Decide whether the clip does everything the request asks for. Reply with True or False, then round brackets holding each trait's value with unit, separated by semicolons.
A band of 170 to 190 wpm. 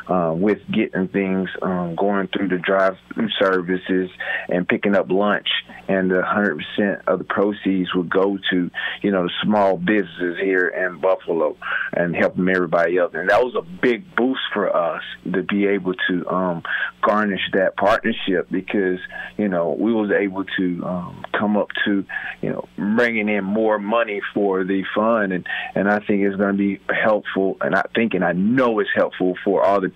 True (180 wpm)